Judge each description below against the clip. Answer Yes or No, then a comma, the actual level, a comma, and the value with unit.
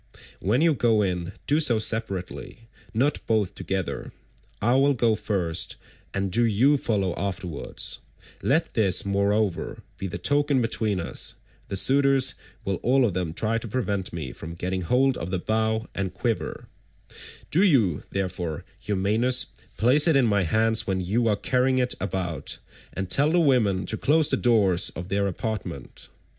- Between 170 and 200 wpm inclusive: No, average, 160 wpm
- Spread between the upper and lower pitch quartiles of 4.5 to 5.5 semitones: Yes, average, 5.0 semitones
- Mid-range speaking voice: No, low, 110 Hz